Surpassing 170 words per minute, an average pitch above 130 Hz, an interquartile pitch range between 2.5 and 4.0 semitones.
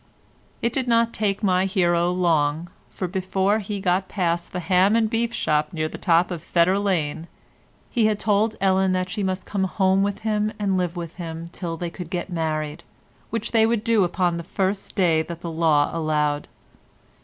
Yes: average, 190 wpm; medium, 185 Hz; average, 3.2 semitones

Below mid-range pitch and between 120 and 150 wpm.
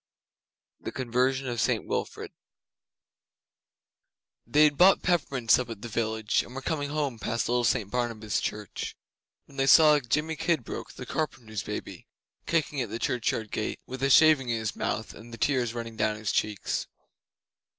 No: low, 120 Hz; average, 160 wpm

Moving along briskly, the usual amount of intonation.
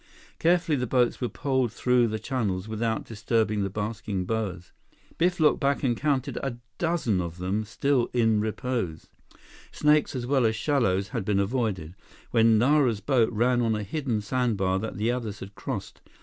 No: average, 170 wpm; average, 3.7 semitones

